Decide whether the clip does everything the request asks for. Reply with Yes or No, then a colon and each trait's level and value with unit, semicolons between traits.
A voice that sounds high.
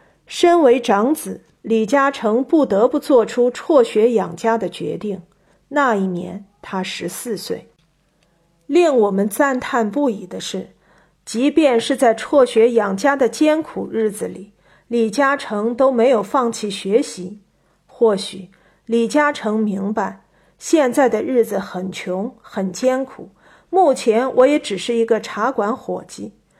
Yes: high, 230 Hz